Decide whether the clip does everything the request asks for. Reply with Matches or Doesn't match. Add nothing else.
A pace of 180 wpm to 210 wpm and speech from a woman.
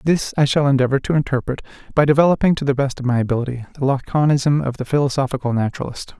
Doesn't match